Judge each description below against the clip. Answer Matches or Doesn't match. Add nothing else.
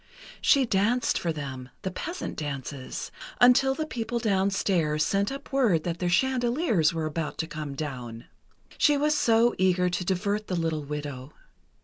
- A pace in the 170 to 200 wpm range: Doesn't match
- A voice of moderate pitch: Matches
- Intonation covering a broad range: Matches